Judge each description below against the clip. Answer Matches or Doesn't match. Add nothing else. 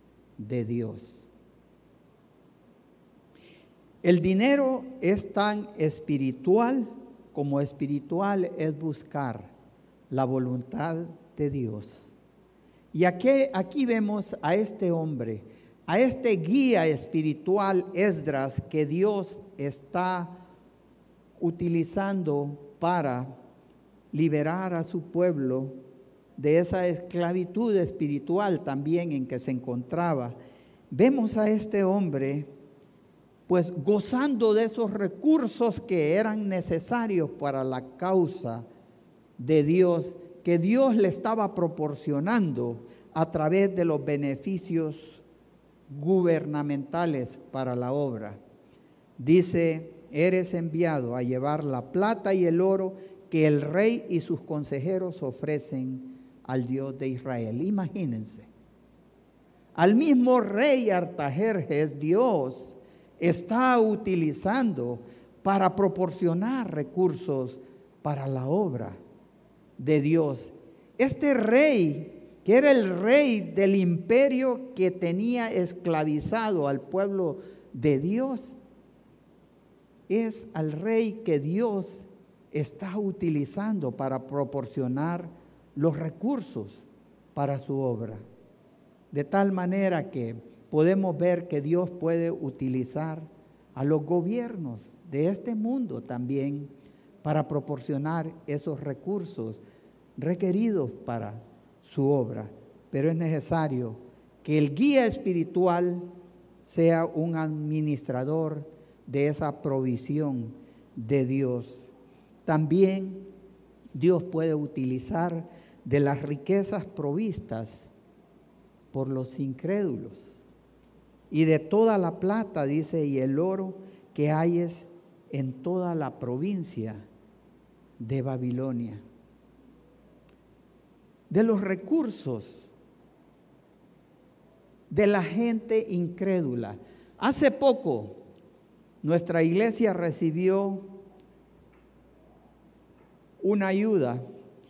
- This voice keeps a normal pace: Doesn't match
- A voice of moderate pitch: Matches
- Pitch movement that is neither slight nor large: Doesn't match